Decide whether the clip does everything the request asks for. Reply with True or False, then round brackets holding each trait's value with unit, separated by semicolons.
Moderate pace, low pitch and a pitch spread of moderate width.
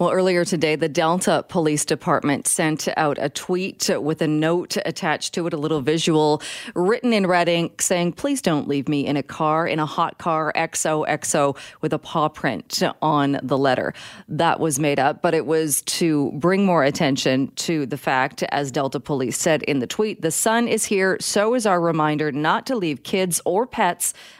False (195 wpm; 160 Hz; 3.2 semitones)